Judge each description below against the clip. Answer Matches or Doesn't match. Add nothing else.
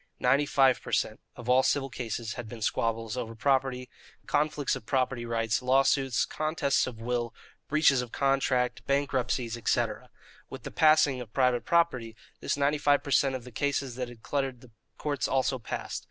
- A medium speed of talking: Matches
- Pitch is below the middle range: Matches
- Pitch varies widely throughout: Doesn't match